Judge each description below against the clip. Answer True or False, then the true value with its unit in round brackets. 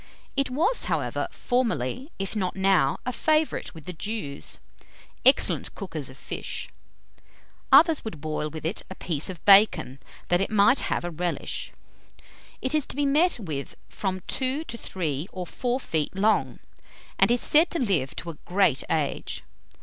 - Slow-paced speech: False (165 wpm)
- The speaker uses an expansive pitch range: True (8.0 semitones)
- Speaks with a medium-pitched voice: False (195 Hz)